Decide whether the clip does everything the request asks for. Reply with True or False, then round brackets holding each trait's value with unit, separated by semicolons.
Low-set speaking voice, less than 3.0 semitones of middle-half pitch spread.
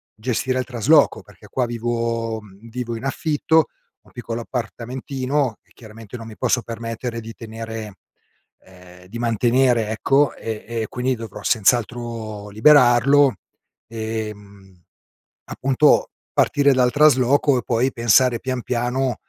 True (115 Hz; 2.6 semitones)